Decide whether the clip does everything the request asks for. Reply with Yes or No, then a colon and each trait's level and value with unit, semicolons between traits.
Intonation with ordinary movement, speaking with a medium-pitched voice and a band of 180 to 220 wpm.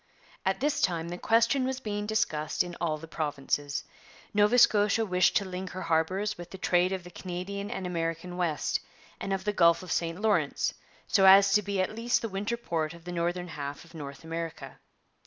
Yes: average, 3.6 semitones; medium, 180 Hz; average, 200 wpm